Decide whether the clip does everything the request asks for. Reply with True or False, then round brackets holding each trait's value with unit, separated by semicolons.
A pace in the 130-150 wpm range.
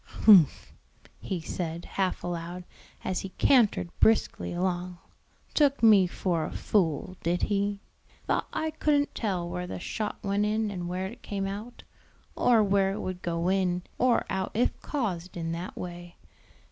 False (160 wpm)